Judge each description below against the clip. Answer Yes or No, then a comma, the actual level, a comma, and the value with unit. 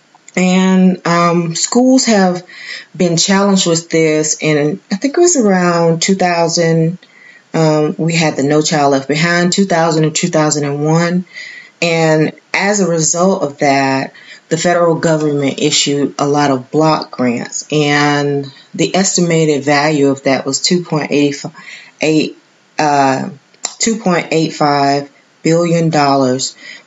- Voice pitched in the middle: Yes, medium, 160 Hz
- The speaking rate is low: Yes, slow, 120 wpm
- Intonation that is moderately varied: Yes, average, 3.3 semitones